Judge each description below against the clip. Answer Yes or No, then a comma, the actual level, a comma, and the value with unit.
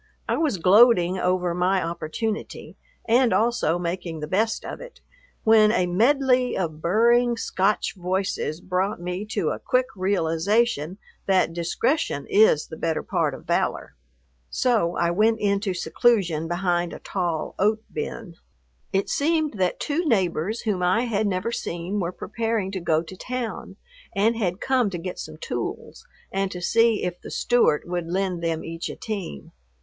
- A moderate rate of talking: Yes, average, 160 wpm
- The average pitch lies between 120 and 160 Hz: No, high, 190 Hz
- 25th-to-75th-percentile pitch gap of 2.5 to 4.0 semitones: No, average, 4.5 semitones